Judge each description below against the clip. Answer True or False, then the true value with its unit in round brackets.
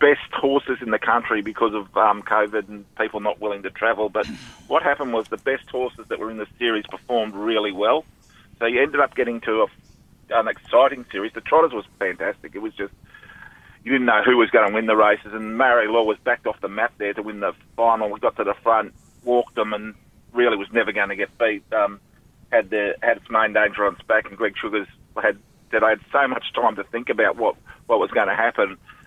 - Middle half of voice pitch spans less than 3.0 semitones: True (2.6 semitones)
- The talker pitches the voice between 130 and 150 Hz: False (110 Hz)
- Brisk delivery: True (235 wpm)